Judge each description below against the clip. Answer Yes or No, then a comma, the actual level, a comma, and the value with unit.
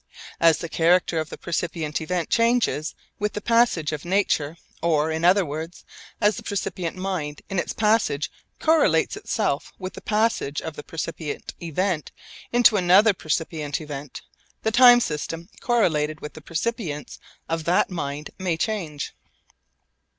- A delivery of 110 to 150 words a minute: Yes, average, 145 wpm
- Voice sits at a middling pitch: Yes, medium, 170 Hz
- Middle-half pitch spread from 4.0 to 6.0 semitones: Yes, average, 4.8 semitones